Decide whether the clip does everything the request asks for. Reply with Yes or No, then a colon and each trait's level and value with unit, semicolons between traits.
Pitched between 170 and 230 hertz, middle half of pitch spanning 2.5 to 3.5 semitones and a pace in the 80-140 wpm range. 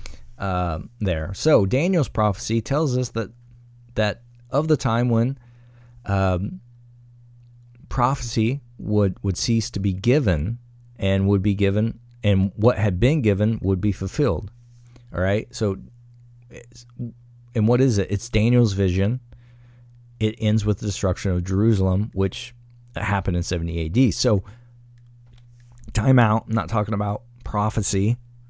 No: low, 115 Hz; average, 3.1 semitones; slow, 135 wpm